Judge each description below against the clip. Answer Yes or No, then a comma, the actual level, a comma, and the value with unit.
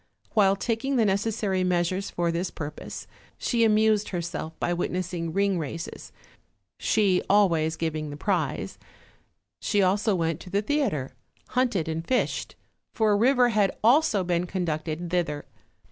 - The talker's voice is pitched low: No, medium, 185 Hz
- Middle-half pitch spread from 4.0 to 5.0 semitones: Yes, average, 4.3 semitones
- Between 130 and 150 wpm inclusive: Yes, average, 145 wpm